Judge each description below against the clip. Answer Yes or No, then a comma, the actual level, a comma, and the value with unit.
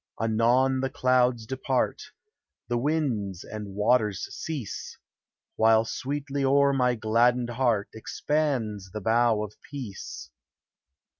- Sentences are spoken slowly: Yes, slow, 105 wpm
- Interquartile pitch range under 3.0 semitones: No, average, 3.5 semitones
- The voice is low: Yes, low, 120 Hz